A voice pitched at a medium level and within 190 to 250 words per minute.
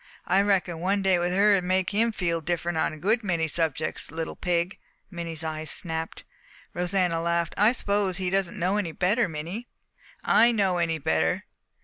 No: medium, 175 Hz; average, 170 wpm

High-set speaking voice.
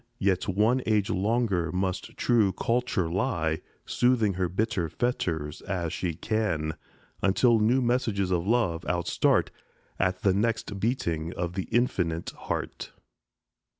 No: very low, 95 Hz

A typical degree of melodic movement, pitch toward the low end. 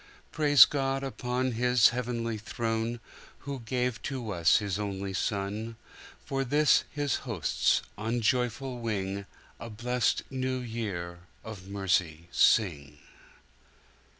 Yes: average, 4.0 semitones; low, 115 Hz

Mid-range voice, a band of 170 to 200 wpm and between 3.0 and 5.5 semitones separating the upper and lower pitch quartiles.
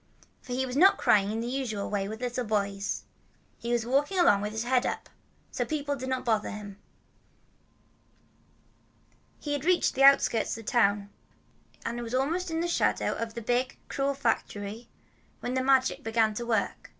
No: high, 240 Hz; average, 180 wpm; average, 3.8 semitones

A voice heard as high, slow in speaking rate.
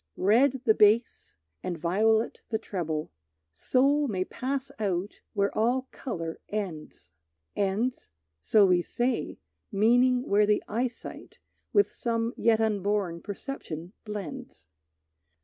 Yes: high, 210 Hz; slow, 115 wpm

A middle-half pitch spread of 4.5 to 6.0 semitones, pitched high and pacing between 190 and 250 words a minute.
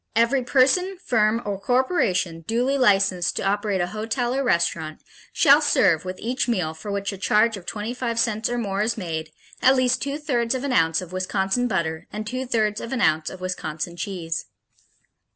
Yes: average, 5.2 semitones; high, 215 Hz; average, 195 wpm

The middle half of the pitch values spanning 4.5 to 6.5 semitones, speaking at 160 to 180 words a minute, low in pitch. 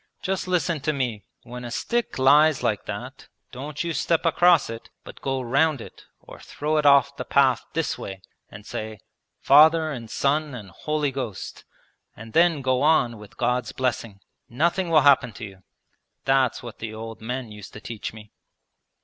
Yes: average, 5.2 semitones; average, 175 wpm; low, 130 Hz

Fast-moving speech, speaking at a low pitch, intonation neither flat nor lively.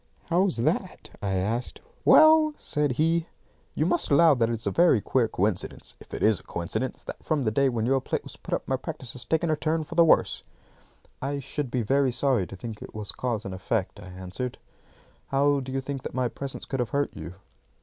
Yes: fast, 220 wpm; low, 130 Hz; average, 5.0 semitones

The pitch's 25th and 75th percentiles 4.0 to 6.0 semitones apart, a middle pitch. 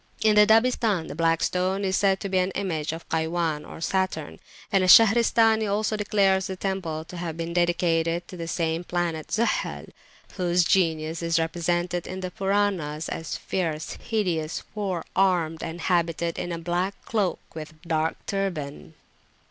No: average, 2.9 semitones; medium, 175 Hz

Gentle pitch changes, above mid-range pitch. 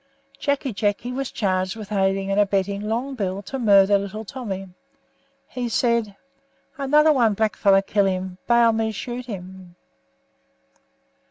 No: average, 3.6 semitones; high, 205 Hz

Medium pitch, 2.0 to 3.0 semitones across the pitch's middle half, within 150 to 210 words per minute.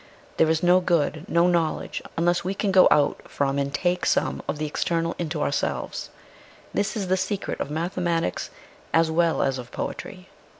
Yes: medium, 170 Hz; average, 2.7 semitones; average, 180 wpm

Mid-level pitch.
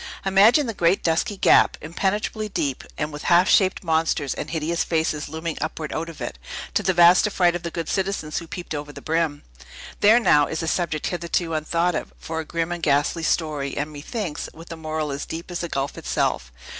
Yes: medium, 165 Hz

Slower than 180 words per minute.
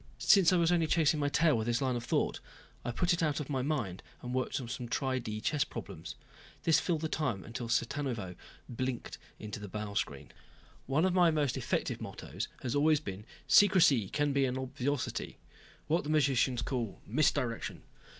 No: average, 190 wpm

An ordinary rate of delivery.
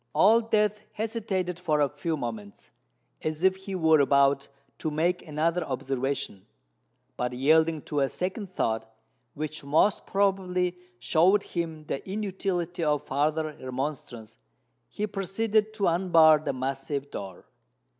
No: slow, 130 wpm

